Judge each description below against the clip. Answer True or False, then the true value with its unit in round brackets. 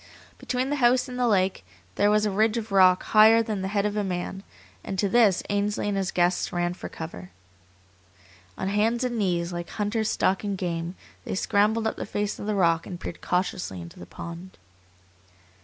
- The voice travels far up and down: False (3.3 semitones)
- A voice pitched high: True (200 Hz)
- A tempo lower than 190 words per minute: False (195 wpm)